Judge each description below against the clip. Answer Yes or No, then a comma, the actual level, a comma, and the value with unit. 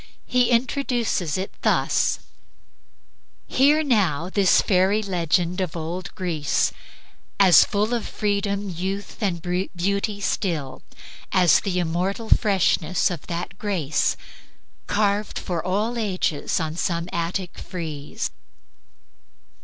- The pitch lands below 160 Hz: No, medium, 185 Hz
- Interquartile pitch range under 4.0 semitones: Yes, average, 3.2 semitones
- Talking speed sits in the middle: No, slow, 105 wpm